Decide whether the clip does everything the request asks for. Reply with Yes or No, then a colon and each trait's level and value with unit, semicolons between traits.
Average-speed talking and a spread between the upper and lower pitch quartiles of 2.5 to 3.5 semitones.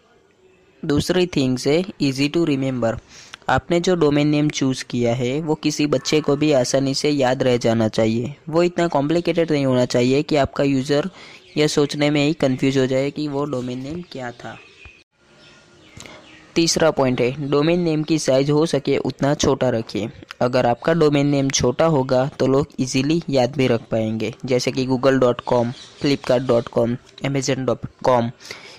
Yes: average, 170 wpm; average, 3.0 semitones